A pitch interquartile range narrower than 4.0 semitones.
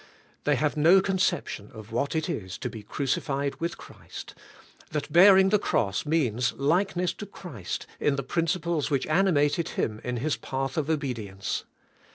No: wide, 5.4 semitones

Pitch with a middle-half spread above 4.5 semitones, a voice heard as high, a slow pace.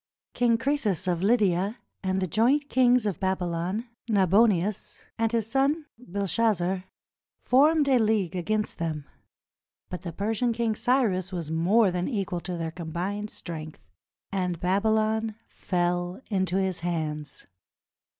No: average, 4.2 semitones; high, 195 Hz; slow, 130 wpm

